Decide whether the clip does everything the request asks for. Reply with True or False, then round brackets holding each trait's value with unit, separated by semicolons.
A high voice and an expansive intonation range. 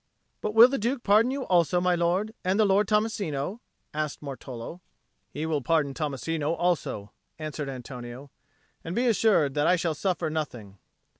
False (165 Hz; 5.9 semitones)